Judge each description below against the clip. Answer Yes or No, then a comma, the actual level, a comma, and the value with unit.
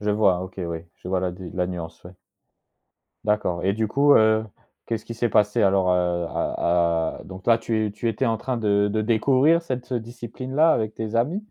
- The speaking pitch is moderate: No, low, 110 Hz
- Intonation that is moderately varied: Yes, average, 4.2 semitones